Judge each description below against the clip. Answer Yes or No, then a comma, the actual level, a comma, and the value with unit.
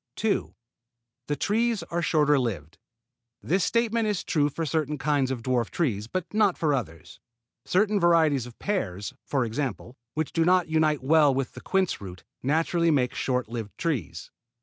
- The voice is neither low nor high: Yes, medium, 150 Hz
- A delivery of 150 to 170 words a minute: Yes, average, 165 wpm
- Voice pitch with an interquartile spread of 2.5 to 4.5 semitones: No, wide, 5.6 semitones